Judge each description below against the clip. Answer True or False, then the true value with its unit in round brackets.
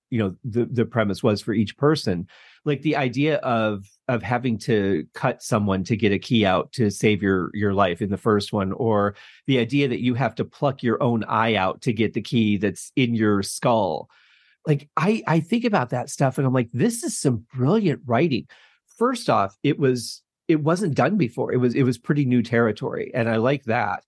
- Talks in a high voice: False (120 Hz)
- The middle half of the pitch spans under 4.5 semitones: False (4.8 semitones)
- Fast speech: True (215 wpm)